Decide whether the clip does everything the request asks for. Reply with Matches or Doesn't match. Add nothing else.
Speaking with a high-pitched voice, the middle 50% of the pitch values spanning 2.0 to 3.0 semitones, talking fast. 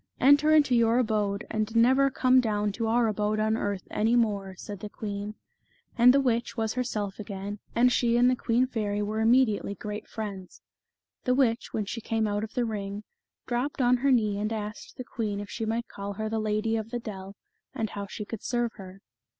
Matches